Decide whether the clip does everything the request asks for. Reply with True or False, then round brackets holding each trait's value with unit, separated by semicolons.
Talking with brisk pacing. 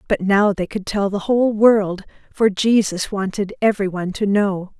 False (175 wpm)